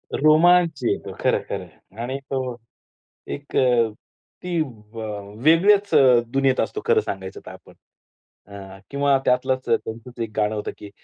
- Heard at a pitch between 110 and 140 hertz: Yes, low, 135 Hz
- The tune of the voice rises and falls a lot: Yes, wide, 6.0 semitones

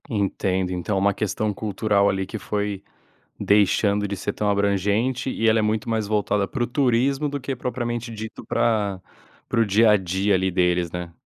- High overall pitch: No, low, 105 Hz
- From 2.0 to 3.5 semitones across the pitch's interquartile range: Yes, average, 2.7 semitones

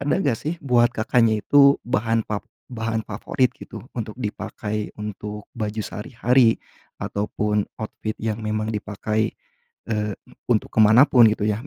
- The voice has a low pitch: Yes, low, 110 Hz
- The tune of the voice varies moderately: No, narrow, 2.2 semitones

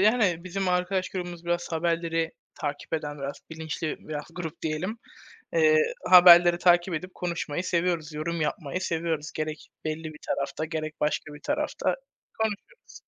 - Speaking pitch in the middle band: Yes, medium, 170 Hz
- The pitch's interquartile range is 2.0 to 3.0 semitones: Yes, average, 2.7 semitones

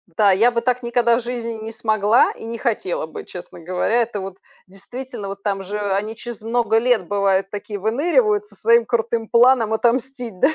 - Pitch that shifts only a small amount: No, average, 3.0 semitones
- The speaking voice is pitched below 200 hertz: No, high, 225 Hz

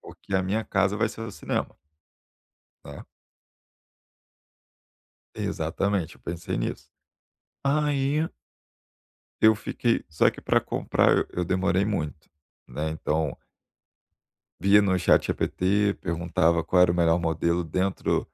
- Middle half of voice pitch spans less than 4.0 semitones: Yes, average, 3.6 semitones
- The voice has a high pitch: No, very low, 95 Hz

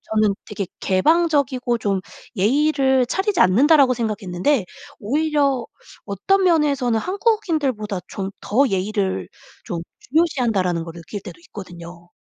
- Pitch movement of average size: No, wide, 7.4 semitones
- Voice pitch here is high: Yes, high, 235 Hz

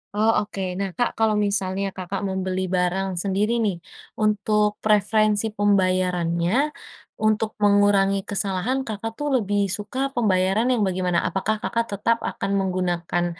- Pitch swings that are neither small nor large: No, narrow, 2.3 semitones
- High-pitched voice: Yes, high, 200 Hz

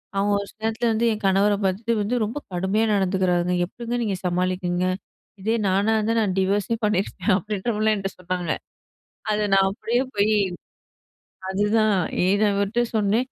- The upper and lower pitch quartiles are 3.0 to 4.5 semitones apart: No, narrow, 2.5 semitones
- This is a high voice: Yes, high, 205 Hz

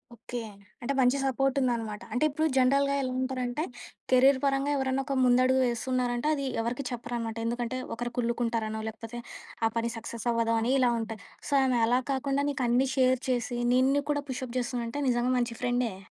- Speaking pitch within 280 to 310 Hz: No, very high, 250 Hz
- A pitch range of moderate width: No, narrow, 2.0 semitones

